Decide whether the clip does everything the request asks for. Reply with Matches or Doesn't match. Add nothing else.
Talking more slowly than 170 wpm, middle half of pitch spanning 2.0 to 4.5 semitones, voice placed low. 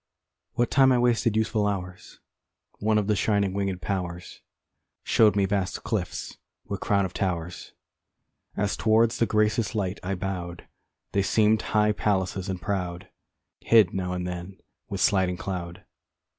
Matches